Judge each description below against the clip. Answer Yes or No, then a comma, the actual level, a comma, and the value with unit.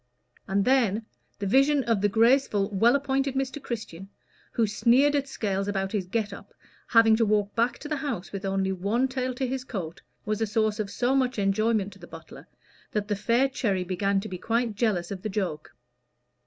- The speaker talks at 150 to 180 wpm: No, average, 200 wpm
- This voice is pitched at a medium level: No, high, 215 Hz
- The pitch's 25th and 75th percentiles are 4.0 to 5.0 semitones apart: Yes, average, 4.3 semitones